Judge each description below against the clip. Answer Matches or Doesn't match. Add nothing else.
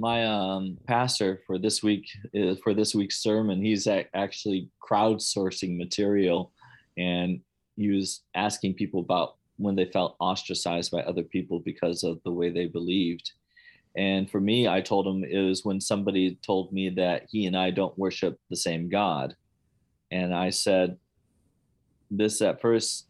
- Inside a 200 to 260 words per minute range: Doesn't match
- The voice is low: Matches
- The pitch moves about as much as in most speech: Doesn't match